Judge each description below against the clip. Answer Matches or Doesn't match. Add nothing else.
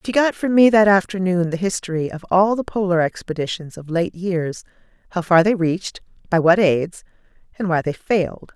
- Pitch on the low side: Doesn't match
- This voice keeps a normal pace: Matches